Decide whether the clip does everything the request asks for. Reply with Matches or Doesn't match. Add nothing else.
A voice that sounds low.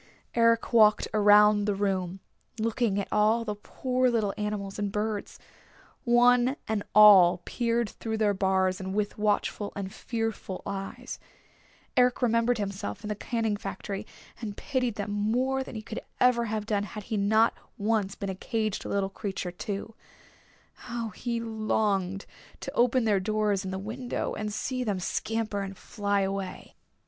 Doesn't match